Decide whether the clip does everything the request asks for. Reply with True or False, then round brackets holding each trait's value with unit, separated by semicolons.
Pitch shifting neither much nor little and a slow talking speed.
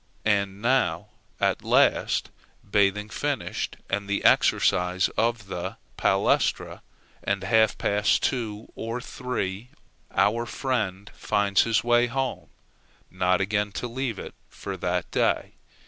True (3.5 semitones; 120 wpm)